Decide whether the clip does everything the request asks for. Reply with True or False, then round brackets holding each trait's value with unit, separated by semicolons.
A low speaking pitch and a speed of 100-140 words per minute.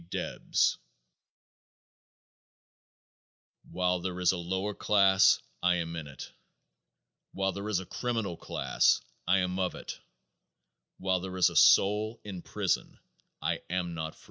True (95 Hz; 135 wpm)